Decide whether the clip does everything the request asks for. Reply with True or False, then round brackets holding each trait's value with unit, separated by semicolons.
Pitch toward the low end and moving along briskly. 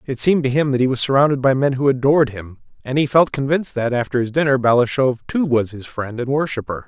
True (130 Hz; 245 wpm)